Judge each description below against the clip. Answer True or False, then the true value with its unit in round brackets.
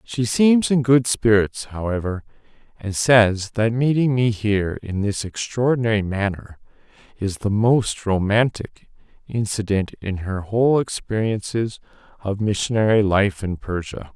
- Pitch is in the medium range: False (110 Hz)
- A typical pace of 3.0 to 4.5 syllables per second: True (4.4 syllables/s)